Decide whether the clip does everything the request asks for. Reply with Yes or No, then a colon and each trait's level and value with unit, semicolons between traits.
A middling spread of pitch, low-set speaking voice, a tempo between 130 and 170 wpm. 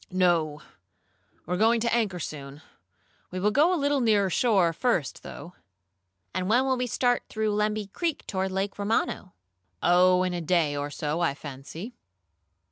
No: average, 5.0 semitones; high, 190 Hz; average, 165 wpm